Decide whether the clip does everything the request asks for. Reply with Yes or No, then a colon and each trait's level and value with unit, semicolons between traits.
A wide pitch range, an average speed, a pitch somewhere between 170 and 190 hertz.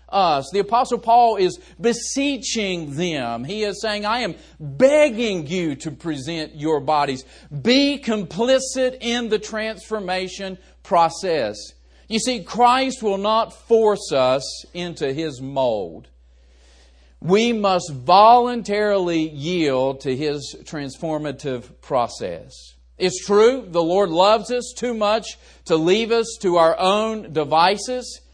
No: wide, 6.6 semitones; slow, 120 wpm; medium, 185 Hz